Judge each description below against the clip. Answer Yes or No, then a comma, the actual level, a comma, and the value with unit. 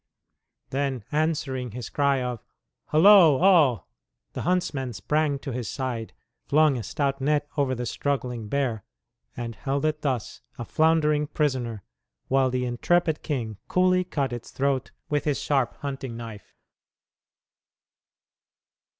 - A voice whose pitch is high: No, low, 135 Hz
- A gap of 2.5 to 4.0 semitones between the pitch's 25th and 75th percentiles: Yes, average, 3.5 semitones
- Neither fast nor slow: No, slow, 130 wpm